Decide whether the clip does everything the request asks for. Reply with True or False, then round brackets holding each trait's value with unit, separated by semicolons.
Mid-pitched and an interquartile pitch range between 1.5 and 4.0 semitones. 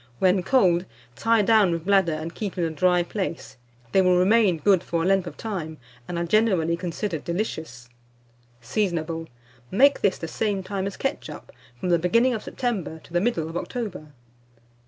True (180 Hz; 3.7 semitones)